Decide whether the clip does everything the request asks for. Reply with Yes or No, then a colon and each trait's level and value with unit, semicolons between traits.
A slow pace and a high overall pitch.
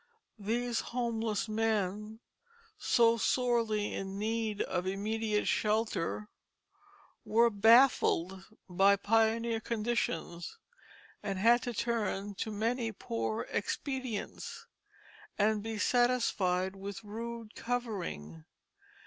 Yes: slow, 90 wpm; high, 215 Hz